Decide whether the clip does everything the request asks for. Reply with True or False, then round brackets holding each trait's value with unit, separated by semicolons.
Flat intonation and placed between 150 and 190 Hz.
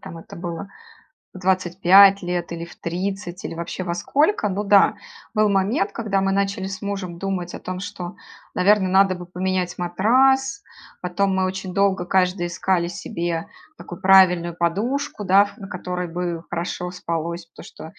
True (2.1 semitones; 185 Hz)